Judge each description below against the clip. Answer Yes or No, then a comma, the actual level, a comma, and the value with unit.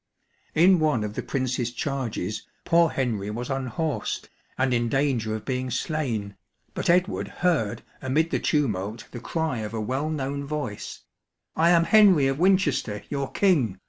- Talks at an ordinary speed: Yes, average, 160 wpm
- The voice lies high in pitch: No, low, 135 Hz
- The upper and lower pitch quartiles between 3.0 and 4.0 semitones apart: No, wide, 5.6 semitones